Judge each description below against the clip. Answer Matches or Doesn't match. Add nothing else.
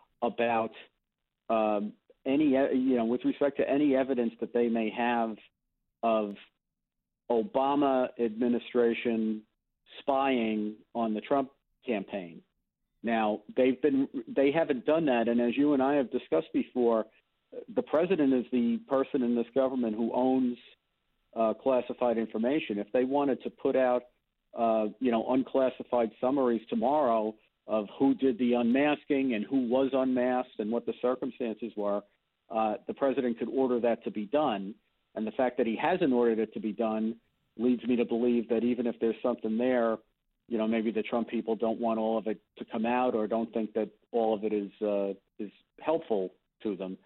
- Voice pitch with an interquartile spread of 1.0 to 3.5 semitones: Matches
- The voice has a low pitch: Matches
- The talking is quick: Doesn't match